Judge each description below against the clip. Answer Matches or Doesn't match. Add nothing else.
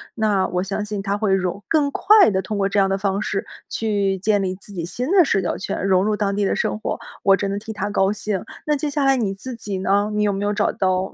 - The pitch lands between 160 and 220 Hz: Matches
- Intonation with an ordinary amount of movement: Doesn't match